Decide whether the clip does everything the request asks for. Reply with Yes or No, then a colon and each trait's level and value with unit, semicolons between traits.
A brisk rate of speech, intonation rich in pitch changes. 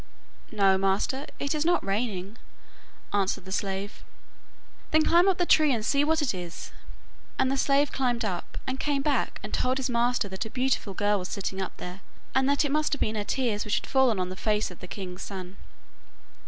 Yes: fast, 210 wpm; wide, 6.0 semitones